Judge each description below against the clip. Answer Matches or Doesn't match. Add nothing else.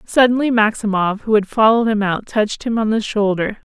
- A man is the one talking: Doesn't match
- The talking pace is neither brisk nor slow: Matches